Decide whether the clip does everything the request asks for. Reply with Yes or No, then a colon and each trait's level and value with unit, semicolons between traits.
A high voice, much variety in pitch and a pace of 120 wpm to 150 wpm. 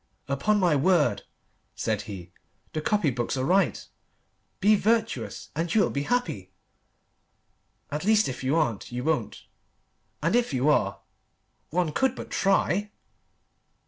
No: medium, 160 Hz; wide, 7.6 semitones; average, 140 wpm